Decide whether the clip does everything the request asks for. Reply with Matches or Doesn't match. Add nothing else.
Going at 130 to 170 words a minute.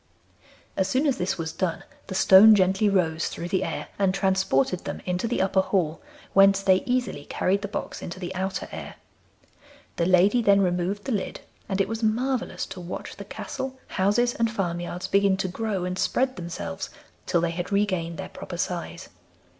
Doesn't match